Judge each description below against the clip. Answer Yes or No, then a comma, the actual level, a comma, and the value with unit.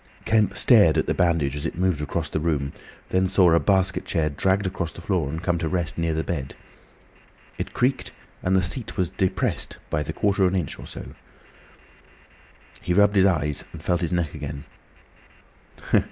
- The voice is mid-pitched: No, very low, 85 Hz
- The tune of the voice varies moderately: Yes, average, 3.2 semitones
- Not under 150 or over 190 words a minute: Yes, average, 185 wpm